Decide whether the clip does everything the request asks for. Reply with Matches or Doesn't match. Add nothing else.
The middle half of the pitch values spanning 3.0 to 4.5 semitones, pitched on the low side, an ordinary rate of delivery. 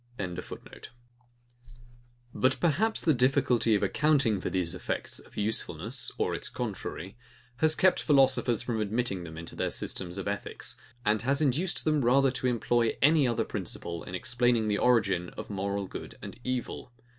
Doesn't match